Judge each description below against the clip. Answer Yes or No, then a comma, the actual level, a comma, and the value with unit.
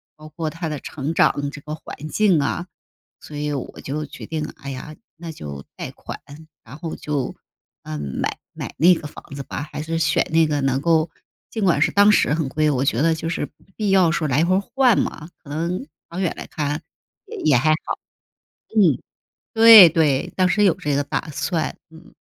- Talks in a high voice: No, medium, 155 Hz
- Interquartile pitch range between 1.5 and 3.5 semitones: Yes, average, 2.8 semitones